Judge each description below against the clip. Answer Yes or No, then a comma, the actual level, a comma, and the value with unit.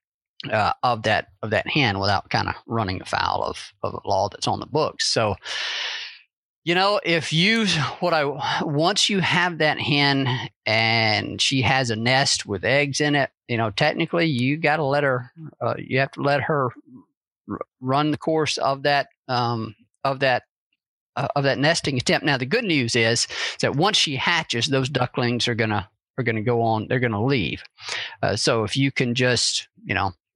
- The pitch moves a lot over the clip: No, average, 4.7 semitones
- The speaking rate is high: No, average, 190 wpm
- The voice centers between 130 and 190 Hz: Yes, medium, 140 Hz